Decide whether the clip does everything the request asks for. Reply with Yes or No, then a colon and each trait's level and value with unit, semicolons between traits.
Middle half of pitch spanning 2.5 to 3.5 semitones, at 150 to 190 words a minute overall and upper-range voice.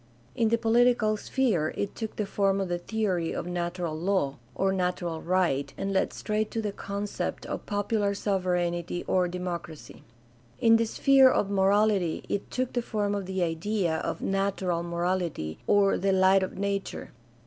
Yes: average, 2.9 semitones; average, 165 wpm; high, 195 Hz